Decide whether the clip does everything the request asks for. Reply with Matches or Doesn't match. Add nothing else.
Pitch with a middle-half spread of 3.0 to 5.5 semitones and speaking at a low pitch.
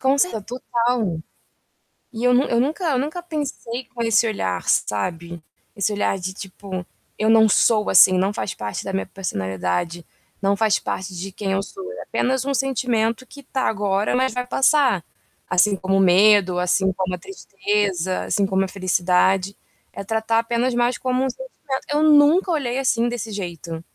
Doesn't match